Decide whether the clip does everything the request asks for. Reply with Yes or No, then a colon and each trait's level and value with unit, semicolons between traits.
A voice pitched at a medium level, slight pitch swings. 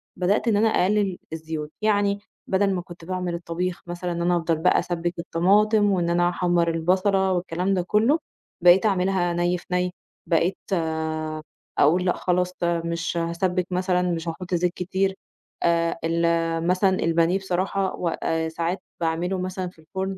Yes: medium, 180 Hz; narrow, 2.0 semitones